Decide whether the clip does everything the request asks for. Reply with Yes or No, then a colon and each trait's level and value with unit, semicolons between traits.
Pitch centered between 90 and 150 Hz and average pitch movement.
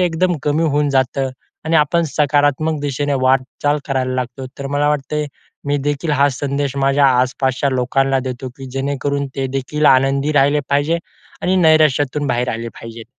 No: medium, 140 Hz; narrow, 1.9 semitones